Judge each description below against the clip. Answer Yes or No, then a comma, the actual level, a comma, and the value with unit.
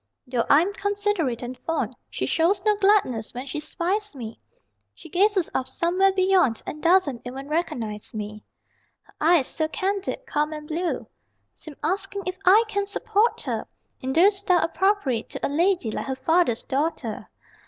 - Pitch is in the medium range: No, very high, 335 Hz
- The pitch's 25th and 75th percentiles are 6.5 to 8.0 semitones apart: Yes, wide, 6.8 semitones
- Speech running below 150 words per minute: No, average, 165 wpm